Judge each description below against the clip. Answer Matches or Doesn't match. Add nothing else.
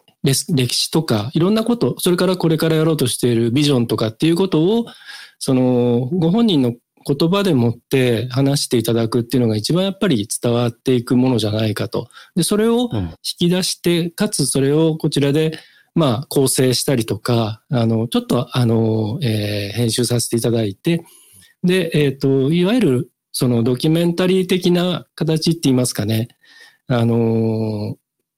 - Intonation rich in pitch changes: Matches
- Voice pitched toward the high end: Doesn't match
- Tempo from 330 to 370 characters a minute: Matches